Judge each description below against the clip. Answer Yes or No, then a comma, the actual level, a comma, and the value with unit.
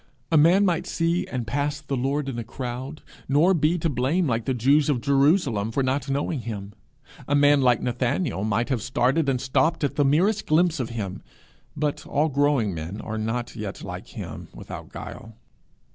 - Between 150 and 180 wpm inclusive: No, average, 190 wpm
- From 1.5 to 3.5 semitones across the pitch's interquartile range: No, average, 4.0 semitones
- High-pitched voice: No, low, 135 Hz